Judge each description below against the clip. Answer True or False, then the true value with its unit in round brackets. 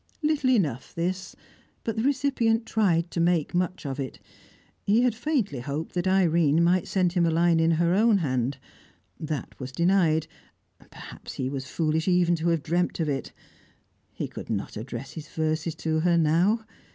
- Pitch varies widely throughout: False (3.5 semitones)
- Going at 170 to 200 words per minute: True (175 wpm)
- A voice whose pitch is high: False (170 Hz)